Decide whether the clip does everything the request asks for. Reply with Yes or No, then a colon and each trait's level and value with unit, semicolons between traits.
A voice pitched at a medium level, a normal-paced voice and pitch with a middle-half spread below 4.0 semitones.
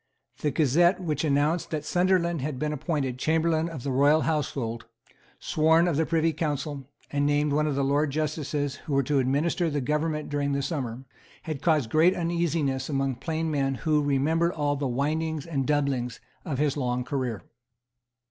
Yes: medium, 150 Hz; average, 170 wpm; average, 2.7 semitones